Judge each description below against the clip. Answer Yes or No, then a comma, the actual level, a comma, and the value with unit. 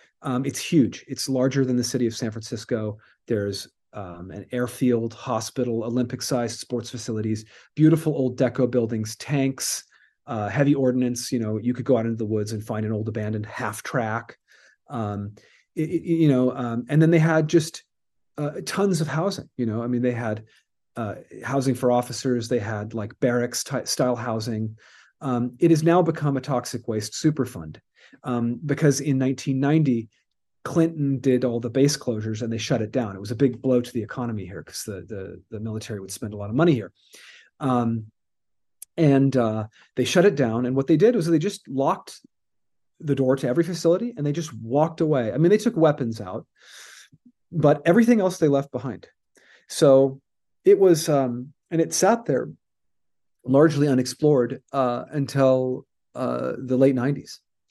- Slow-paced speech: No, average, 180 wpm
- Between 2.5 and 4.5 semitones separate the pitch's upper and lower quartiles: Yes, average, 4.0 semitones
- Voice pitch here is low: Yes, low, 125 Hz